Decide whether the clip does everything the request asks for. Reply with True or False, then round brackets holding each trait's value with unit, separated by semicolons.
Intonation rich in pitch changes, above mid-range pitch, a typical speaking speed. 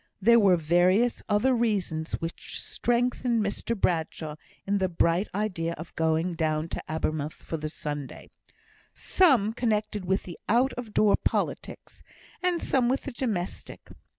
True (6.1 semitones; 195 Hz; 145 wpm)